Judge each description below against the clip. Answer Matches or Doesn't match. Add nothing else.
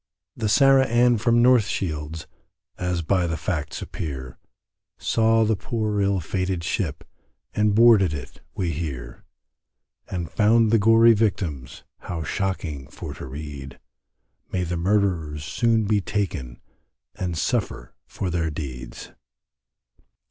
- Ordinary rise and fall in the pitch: Doesn't match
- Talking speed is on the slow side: Matches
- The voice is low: Matches